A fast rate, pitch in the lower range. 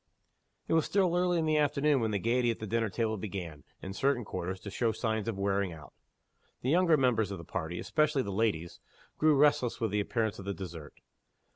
Yes: fast, 215 wpm; low, 110 Hz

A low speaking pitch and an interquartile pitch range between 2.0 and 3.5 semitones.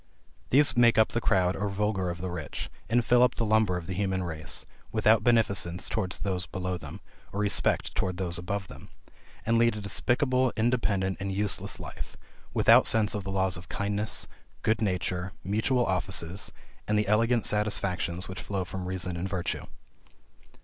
Yes: low, 100 Hz; average, 3.2 semitones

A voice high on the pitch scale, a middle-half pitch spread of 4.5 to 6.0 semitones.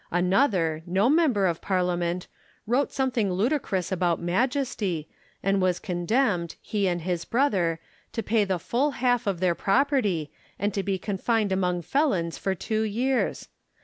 Yes: high, 195 Hz; average, 5.2 semitones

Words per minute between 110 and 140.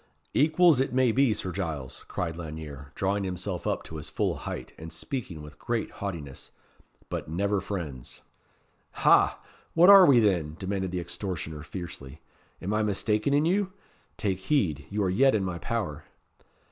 No: average, 160 wpm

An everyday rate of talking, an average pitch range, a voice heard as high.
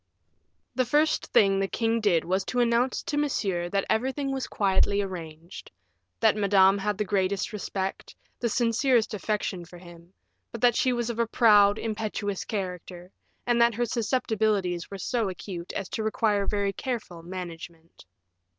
Yes: average, 160 wpm; average, 3.9 semitones; high, 205 Hz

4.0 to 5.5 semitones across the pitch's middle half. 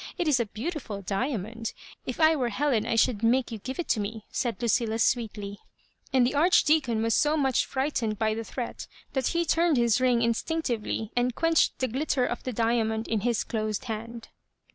No: average, 3.2 semitones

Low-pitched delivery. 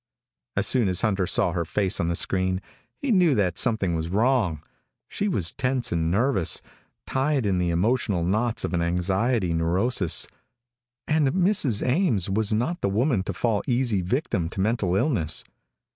Yes: low, 100 Hz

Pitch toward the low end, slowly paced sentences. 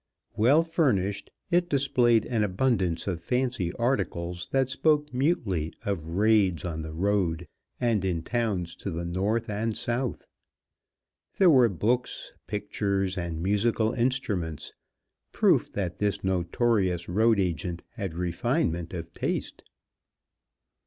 Yes: low, 100 Hz; slow, 120 wpm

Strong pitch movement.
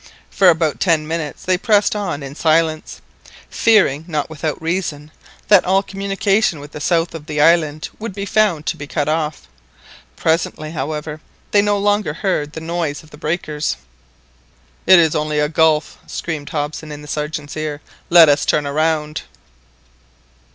No: average, 3.0 semitones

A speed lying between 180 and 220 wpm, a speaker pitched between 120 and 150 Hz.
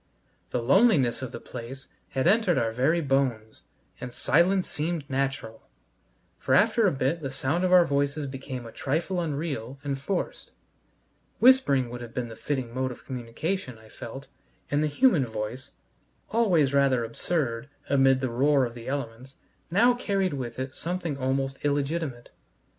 No: average, 160 wpm; low, 135 Hz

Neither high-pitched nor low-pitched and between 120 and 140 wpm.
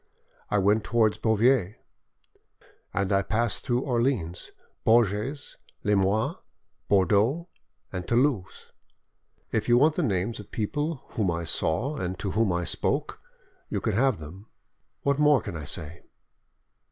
No: low, 105 Hz; slow, 135 wpm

